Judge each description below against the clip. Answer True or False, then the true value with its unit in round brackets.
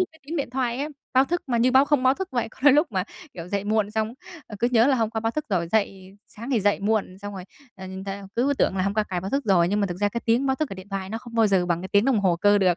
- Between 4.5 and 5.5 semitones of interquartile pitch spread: True (4.8 semitones)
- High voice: True (215 Hz)